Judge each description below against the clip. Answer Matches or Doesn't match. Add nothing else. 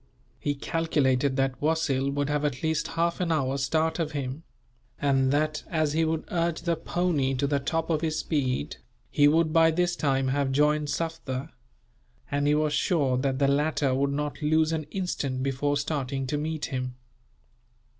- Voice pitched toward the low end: Doesn't match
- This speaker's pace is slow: Doesn't match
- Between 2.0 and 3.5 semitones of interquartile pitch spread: Matches